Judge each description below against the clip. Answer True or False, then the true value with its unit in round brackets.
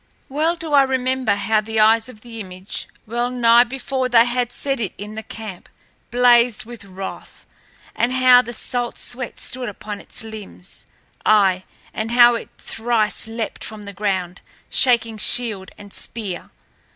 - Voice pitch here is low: False (230 Hz)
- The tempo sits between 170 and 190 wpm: False (160 wpm)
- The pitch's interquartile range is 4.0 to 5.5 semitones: False (2.8 semitones)